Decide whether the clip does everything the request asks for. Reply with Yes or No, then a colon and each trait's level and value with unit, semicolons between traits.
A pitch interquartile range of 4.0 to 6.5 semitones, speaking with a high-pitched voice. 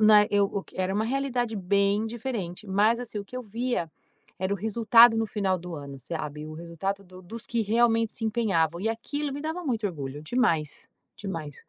Yes: average, 4.6 semitones; high, 205 Hz